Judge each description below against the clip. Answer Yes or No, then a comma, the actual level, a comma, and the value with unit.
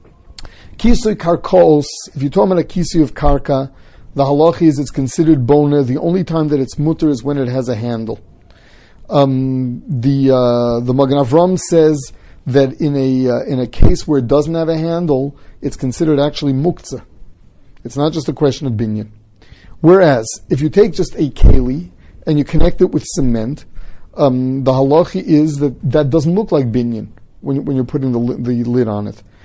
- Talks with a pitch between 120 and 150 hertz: Yes, medium, 140 Hz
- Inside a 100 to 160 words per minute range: No, average, 180 wpm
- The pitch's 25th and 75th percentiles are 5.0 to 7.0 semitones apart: No, average, 4.0 semitones